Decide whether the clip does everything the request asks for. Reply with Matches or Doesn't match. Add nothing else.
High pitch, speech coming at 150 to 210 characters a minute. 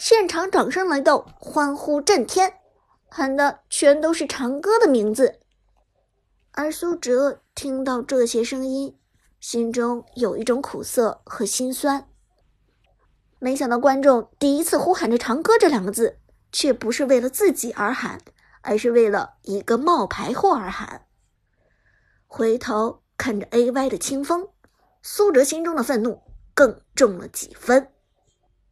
Matches